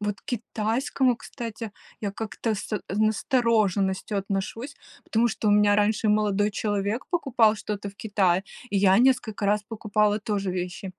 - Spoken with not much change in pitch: Yes, narrow, 1.9 semitones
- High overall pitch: Yes, high, 210 Hz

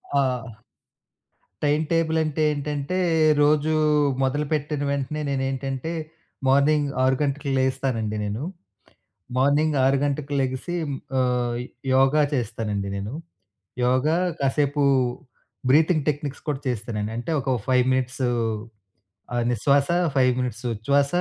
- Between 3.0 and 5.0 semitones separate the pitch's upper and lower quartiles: No, narrow, 2.6 semitones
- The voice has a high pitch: No, low, 135 Hz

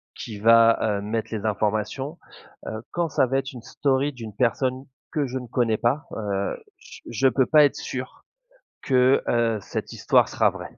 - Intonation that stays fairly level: No, average, 3.4 semitones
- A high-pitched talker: No, low, 120 Hz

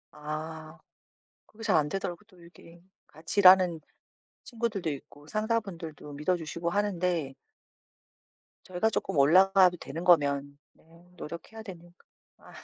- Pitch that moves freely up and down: No, average, 3.7 semitones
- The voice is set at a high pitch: No, medium, 175 Hz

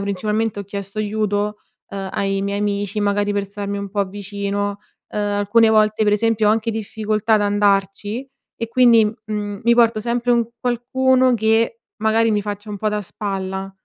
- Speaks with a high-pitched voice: Yes, high, 210 Hz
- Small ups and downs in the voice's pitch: Yes, narrow, 1.7 semitones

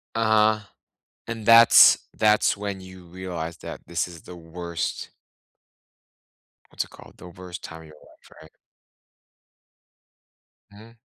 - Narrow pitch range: No, average, 3.9 semitones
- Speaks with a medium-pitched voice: No, very low, 95 Hz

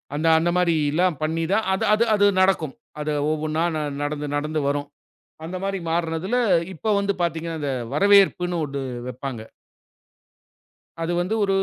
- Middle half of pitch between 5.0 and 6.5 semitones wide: No, average, 3.8 semitones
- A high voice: No, medium, 165 Hz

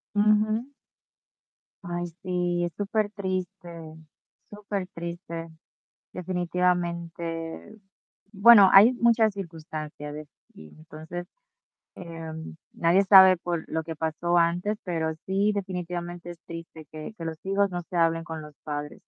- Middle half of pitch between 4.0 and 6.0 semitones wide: No, average, 2.9 semitones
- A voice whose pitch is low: No, medium, 175 Hz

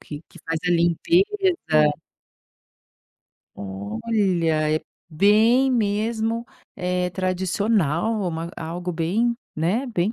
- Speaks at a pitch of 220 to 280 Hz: No, medium, 185 Hz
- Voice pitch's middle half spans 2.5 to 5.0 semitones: No, wide, 5.5 semitones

